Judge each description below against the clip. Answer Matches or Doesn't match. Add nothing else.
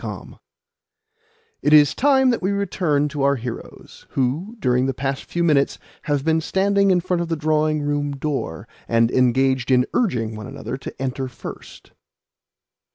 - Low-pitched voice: Doesn't match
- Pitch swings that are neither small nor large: Matches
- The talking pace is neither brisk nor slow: Matches